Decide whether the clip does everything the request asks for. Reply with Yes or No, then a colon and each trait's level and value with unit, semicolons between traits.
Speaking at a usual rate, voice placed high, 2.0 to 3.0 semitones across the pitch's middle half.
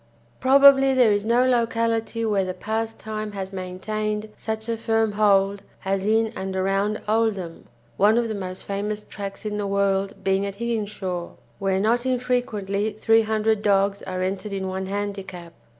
Yes: average, 160 wpm; high, 210 Hz; narrow, 2.4 semitones